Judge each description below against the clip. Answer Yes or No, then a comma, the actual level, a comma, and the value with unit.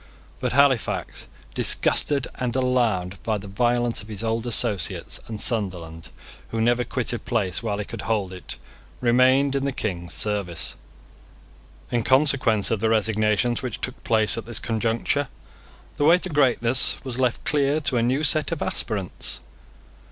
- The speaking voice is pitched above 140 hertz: No, low, 115 Hz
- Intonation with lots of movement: No, average, 3.5 semitones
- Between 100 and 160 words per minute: Yes, average, 155 wpm